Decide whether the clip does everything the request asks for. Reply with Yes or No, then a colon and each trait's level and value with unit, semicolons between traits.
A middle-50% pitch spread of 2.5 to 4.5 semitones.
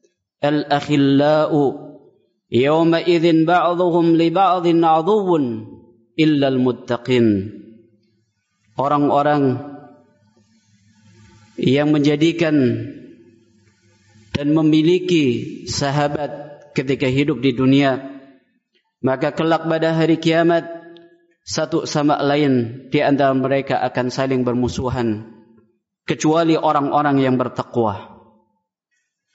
No: average, 5.2 semitones